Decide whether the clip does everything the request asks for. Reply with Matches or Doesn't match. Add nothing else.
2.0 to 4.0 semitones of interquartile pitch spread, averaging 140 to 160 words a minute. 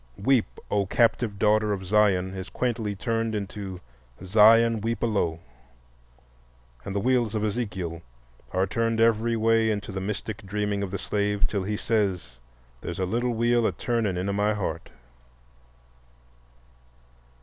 Matches